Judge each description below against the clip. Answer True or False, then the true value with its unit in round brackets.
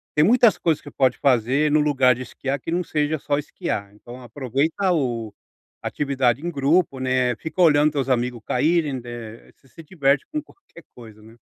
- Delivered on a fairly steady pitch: False (3.8 semitones)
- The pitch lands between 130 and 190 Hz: True (140 Hz)